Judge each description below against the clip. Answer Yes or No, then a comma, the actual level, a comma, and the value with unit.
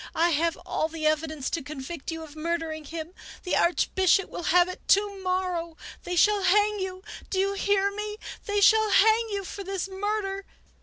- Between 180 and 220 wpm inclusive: Yes, average, 185 wpm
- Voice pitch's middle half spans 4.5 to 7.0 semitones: No, average, 3.5 semitones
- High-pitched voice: Yes, very high, 370 Hz